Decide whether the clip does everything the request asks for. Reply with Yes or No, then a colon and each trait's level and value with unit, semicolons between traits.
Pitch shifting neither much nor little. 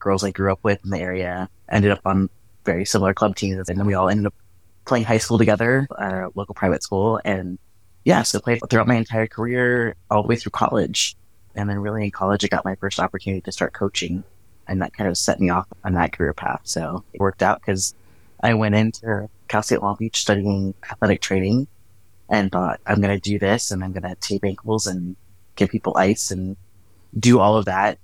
No: narrow, 2.2 semitones